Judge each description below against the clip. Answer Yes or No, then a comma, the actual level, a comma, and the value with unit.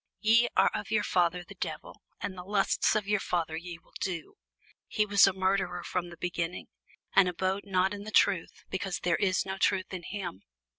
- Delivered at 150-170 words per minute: No, average, 200 wpm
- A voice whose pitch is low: No, medium, 185 Hz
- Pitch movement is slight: Yes, narrow, 2.2 semitones